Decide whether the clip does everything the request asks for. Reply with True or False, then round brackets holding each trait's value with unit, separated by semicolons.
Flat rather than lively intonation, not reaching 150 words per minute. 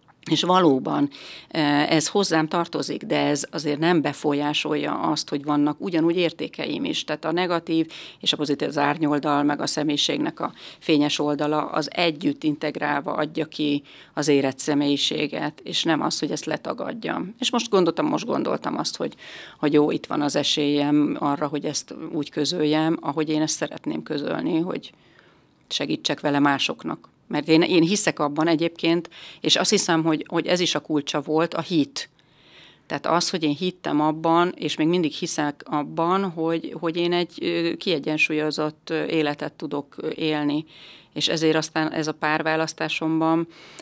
False (1.8 semitones; 155 wpm)